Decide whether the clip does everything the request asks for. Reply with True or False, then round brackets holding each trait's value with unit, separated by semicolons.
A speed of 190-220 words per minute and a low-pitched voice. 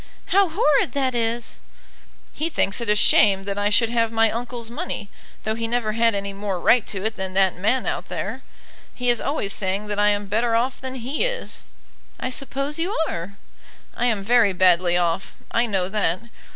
False (195 wpm; 225 Hz)